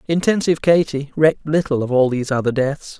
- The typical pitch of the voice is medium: Yes, medium, 145 Hz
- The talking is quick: No, average, 180 wpm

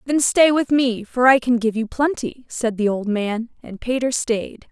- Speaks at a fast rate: Yes, fast, 215 wpm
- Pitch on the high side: Yes, high, 240 Hz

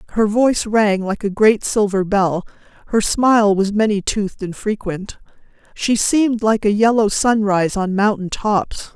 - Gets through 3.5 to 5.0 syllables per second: Yes, 4.6 syllables/s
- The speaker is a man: No, female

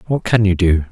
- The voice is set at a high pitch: No, low, 100 Hz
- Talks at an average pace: No, fast, 260 wpm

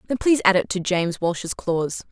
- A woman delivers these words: Yes, female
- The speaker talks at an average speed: No, fast, 225 wpm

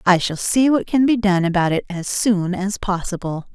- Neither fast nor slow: No, fast, 220 wpm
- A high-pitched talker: Yes, high, 195 Hz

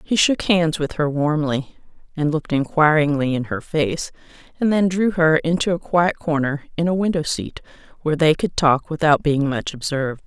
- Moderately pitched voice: Yes, medium, 155 Hz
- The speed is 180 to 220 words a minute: Yes, average, 185 wpm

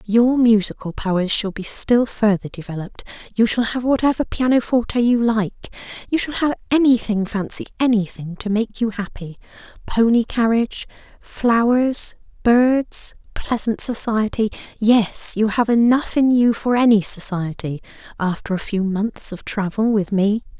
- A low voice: No, high, 220 Hz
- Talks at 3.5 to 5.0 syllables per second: Yes, 4.5 syllables/s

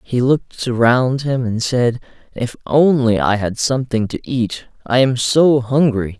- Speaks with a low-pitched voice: Yes, low, 125 Hz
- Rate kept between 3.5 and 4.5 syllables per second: Yes, 4.2 syllables/s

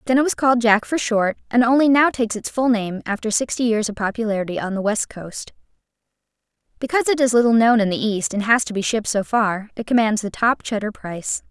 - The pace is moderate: No, fast, 230 wpm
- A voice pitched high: Yes, high, 225 Hz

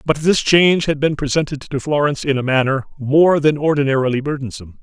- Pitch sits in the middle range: Yes, medium, 145 Hz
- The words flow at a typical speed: Yes, average, 185 wpm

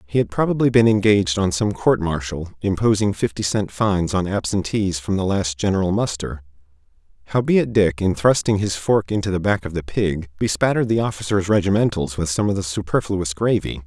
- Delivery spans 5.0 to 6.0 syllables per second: Yes, 5.5 syllables/s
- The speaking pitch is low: Yes, very low, 95 Hz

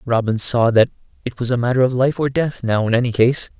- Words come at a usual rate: No, fast, 250 wpm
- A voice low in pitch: Yes, low, 125 Hz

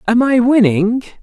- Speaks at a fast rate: No, average, 145 wpm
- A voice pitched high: Yes, high, 230 Hz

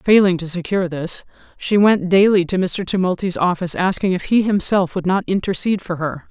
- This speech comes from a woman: Yes, female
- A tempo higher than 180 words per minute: Yes, average, 190 wpm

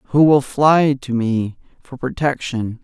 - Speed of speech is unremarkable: Yes, average, 150 wpm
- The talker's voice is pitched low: Yes, low, 130 Hz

